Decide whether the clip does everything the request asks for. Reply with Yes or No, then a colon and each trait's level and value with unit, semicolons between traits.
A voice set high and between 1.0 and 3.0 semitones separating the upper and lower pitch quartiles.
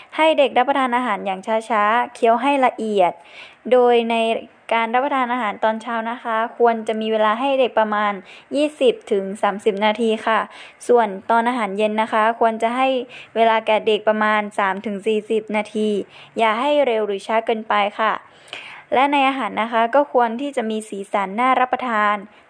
Yes: high, 225 Hz; narrow, 2.6 semitones